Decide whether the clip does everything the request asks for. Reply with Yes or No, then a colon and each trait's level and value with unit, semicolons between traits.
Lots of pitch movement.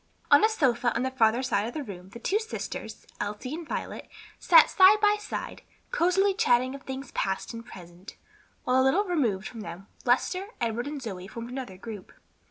Yes: wide, 7.3 semitones